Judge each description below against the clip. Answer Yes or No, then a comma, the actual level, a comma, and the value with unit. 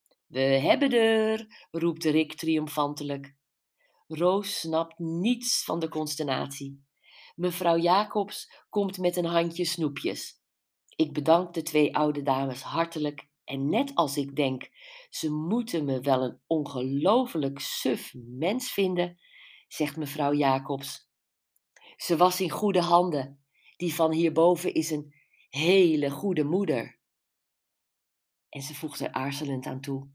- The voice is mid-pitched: Yes, medium, 155 Hz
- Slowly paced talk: Yes, slow, 125 wpm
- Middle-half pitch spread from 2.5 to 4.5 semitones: Yes, average, 3.9 semitones